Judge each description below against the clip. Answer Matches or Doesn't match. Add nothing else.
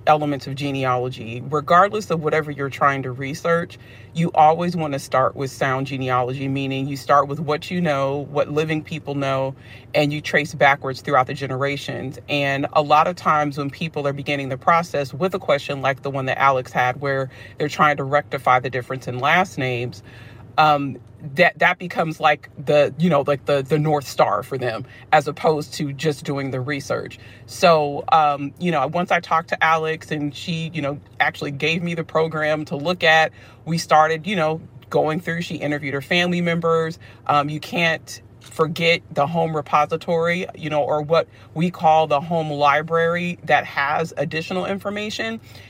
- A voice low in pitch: Doesn't match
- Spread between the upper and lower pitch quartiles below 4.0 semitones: Matches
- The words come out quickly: Doesn't match